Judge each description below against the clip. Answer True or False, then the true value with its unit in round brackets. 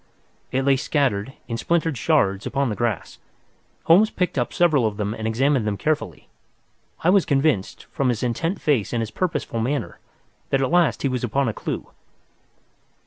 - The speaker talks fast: False (175 wpm)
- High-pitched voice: False (135 Hz)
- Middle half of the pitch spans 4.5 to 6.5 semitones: True (5.5 semitones)